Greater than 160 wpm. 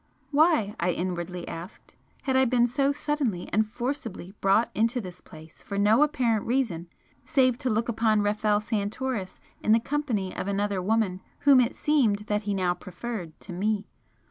Yes: average, 170 wpm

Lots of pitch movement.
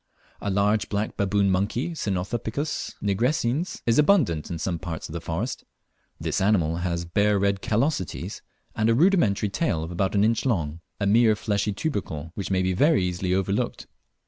No: average, 4.2 semitones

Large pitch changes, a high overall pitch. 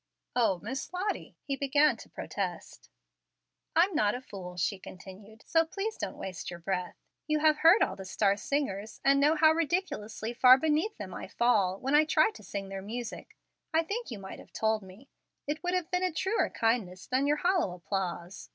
Yes: wide, 8.3 semitones; very high, 250 Hz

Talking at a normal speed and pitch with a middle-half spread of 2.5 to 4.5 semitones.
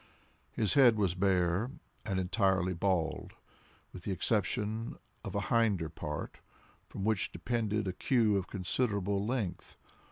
No: slow, 130 wpm; average, 3.3 semitones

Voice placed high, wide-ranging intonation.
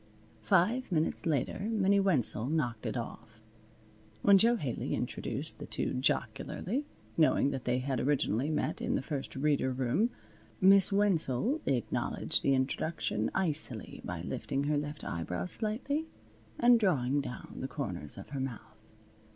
No: medium, 140 Hz; wide, 7.5 semitones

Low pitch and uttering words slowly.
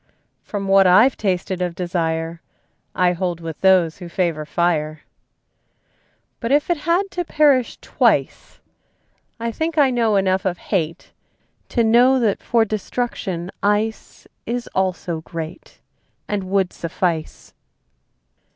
No: high, 190 Hz; slow, 125 wpm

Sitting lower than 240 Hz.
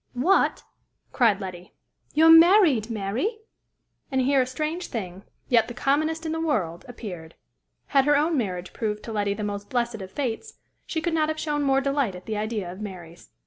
No: high, 245 Hz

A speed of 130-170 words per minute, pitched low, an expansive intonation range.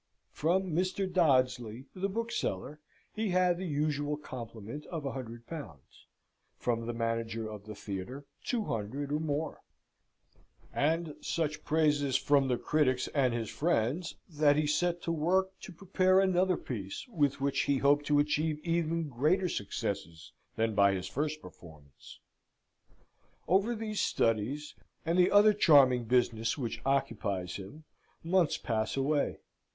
No: average, 140 wpm; medium, 145 Hz; wide, 6.4 semitones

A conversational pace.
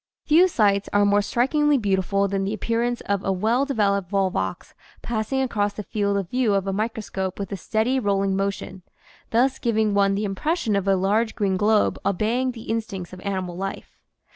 Yes: average, 185 wpm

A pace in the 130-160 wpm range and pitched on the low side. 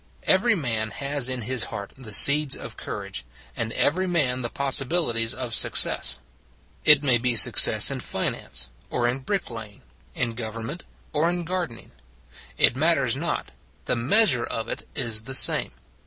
Yes: average, 155 wpm; low, 130 Hz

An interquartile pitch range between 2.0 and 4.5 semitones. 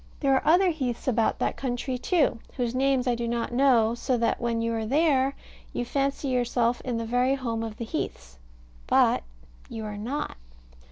Yes: average, 2.8 semitones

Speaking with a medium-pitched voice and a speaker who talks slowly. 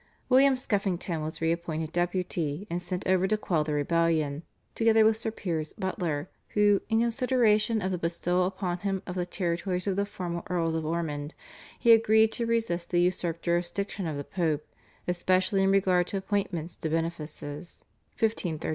No: medium, 180 Hz; average, 165 wpm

